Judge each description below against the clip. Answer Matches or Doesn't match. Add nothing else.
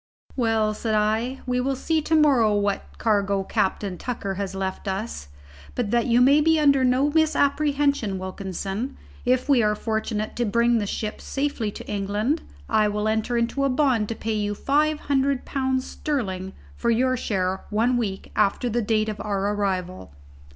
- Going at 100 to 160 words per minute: Doesn't match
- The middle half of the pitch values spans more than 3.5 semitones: Matches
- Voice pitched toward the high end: Matches